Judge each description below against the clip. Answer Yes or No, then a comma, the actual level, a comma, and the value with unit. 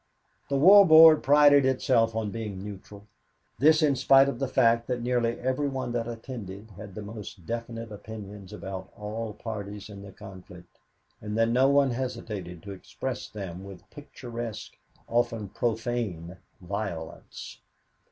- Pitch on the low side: Yes, low, 115 Hz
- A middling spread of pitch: Yes, average, 4.2 semitones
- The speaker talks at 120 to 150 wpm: Yes, average, 145 wpm